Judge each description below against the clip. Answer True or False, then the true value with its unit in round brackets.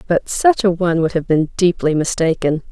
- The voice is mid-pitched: True (175 Hz)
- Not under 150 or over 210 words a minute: True (200 wpm)